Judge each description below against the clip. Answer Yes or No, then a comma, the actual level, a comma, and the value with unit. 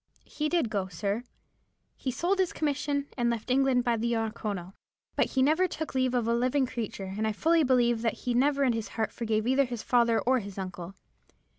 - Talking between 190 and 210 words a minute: Yes, average, 200 wpm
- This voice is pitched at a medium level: No, high, 240 Hz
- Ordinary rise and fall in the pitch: Yes, average, 3.7 semitones